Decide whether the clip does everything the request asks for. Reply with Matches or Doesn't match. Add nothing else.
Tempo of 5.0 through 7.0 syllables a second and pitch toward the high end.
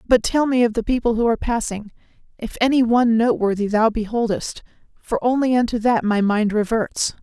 Matches